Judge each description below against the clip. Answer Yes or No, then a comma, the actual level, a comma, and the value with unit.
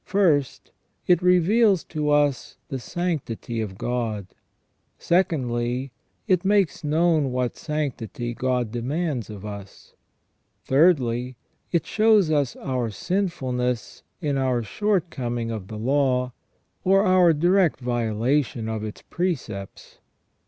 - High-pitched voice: No, low, 135 Hz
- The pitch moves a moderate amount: No, wide, 6.4 semitones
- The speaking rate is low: Yes, slow, 110 wpm